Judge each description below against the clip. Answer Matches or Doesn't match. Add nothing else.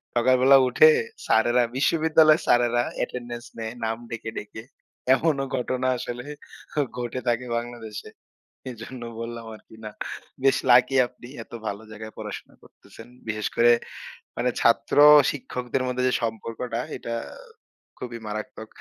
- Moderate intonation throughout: Doesn't match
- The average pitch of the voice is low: Matches